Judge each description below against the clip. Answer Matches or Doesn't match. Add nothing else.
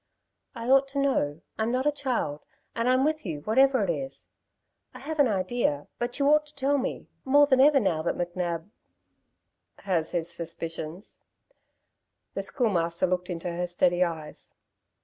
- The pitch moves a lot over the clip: Matches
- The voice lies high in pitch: Matches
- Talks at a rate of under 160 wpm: Doesn't match